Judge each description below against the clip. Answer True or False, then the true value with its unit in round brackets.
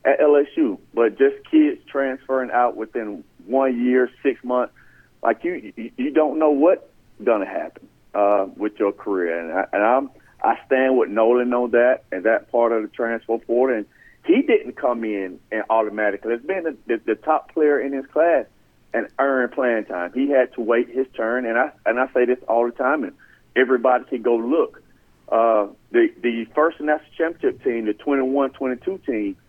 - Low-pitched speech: True (125 Hz)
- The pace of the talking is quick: False (195 wpm)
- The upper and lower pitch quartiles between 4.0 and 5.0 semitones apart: True (4.4 semitones)